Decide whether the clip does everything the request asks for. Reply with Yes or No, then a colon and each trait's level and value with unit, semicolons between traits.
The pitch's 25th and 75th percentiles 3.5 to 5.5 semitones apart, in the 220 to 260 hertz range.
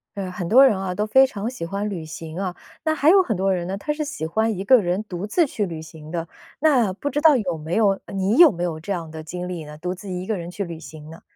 No: average, 4.6 semitones; high, 190 Hz